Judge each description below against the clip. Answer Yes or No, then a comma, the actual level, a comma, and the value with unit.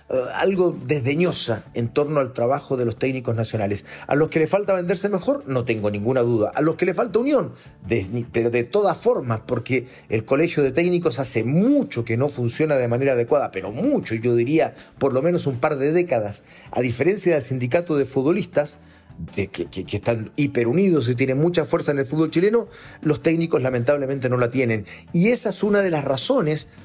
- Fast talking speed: Yes, fast, 200 wpm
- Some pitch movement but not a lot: No, wide, 6.0 semitones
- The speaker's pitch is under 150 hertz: Yes, medium, 140 Hz